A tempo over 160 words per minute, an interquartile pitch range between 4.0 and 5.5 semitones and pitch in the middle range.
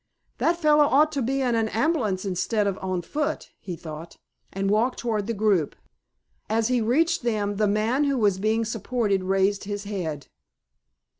No: average, 170 wpm; average, 4.4 semitones; high, 215 Hz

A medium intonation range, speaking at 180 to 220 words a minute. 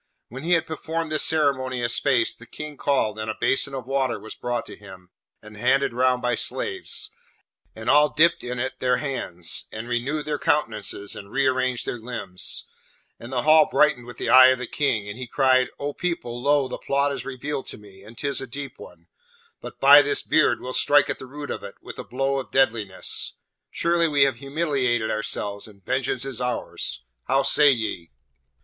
Yes: average, 3.3 semitones; average, 200 wpm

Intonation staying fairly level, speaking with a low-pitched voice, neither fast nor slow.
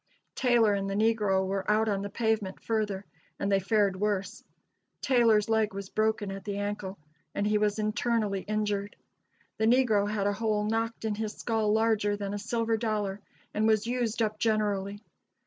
No: narrow, 1.6 semitones; high, 210 Hz; average, 175 wpm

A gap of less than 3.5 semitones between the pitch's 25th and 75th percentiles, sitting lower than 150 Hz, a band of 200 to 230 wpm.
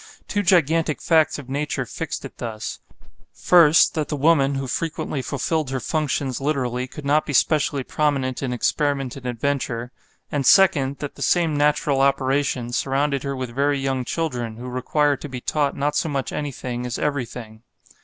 No: average, 2.7 semitones; medium, 140 Hz; average, 170 wpm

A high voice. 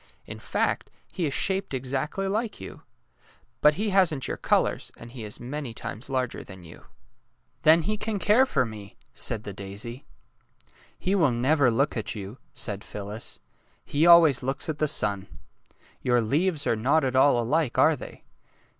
No: low, 135 Hz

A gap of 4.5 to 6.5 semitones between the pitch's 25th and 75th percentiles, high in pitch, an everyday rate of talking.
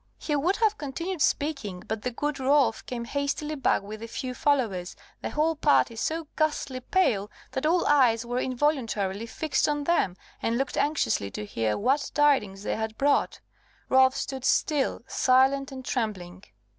Yes: average, 4.8 semitones; very high, 265 Hz; average, 165 wpm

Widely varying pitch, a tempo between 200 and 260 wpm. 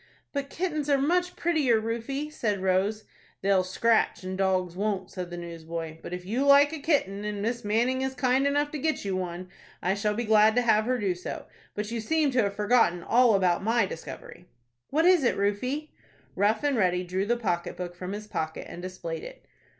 Yes: wide, 6.0 semitones; fast, 205 wpm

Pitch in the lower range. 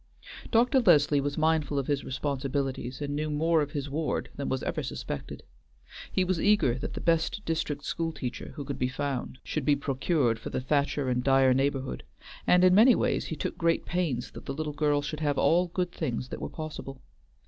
No: medium, 145 Hz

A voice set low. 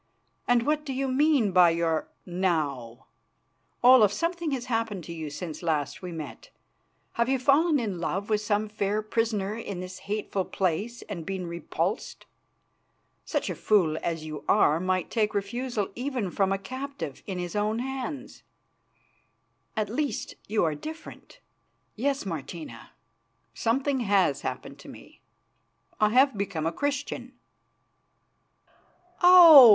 No: high, 210 Hz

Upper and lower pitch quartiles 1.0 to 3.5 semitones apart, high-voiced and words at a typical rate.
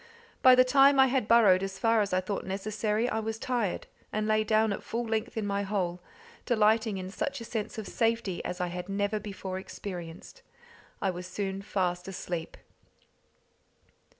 Yes: average, 3.1 semitones; high, 210 Hz; average, 175 wpm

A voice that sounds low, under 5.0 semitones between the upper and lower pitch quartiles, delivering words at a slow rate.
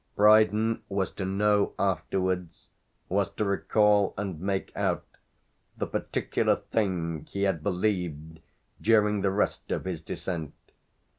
Yes: very low, 95 Hz; average, 2.7 semitones; slow, 125 wpm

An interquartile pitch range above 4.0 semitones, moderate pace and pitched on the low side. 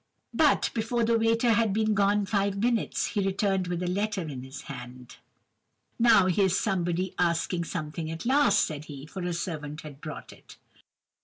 No: average, 4.9 semitones; average, 170 wpm; medium, 185 Hz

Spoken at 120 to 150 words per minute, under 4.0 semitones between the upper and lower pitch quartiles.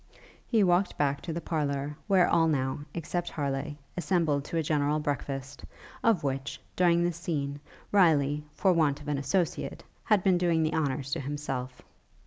No: average, 165 wpm; average, 3.6 semitones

